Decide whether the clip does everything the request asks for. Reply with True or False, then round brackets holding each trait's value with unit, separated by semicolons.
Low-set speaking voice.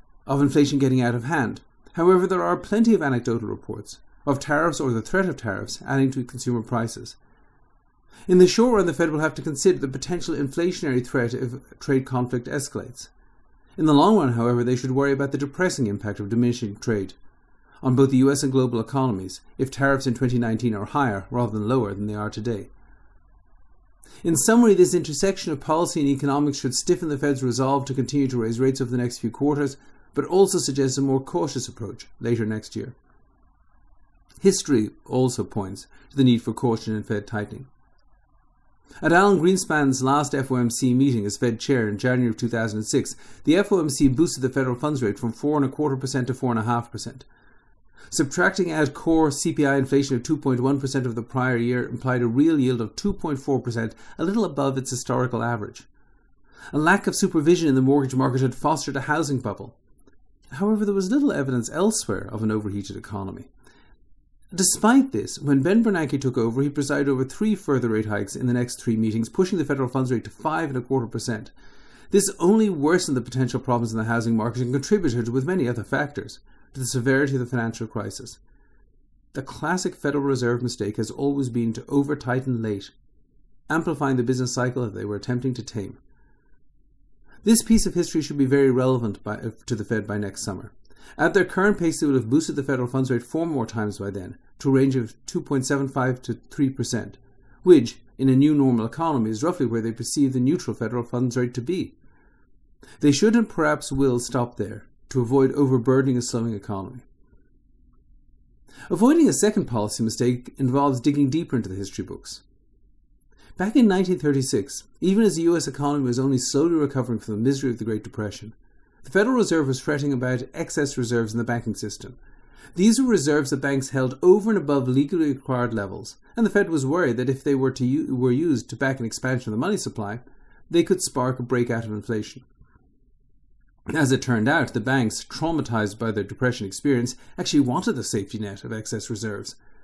True (130 Hz)